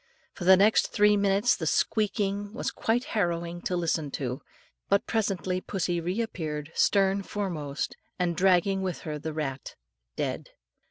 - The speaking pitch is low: No, medium, 185 Hz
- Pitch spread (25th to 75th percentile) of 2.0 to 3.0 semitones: No, average, 3.7 semitones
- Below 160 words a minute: Yes, average, 150 wpm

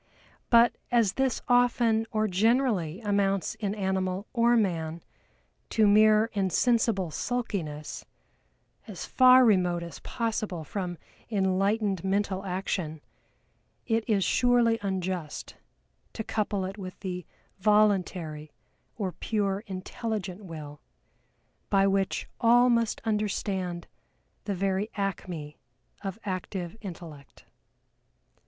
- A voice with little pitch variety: No, average, 3.3 semitones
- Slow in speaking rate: Yes, slow, 105 wpm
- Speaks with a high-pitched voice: Yes, high, 195 Hz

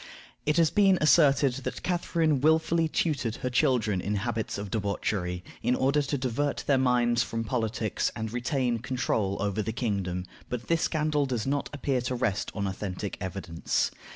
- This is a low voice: Yes, low, 125 Hz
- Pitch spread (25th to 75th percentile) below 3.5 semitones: No, wide, 5.4 semitones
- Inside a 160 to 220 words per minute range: Yes, average, 165 wpm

